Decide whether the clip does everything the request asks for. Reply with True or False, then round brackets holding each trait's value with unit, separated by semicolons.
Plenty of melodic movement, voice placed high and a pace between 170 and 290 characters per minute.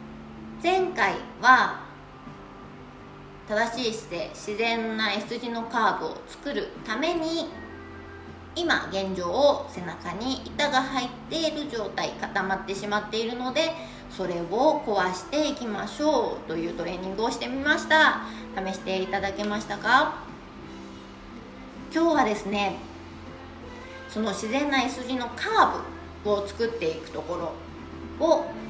True (6.4 semitones; 225 Hz; 245 characters per minute)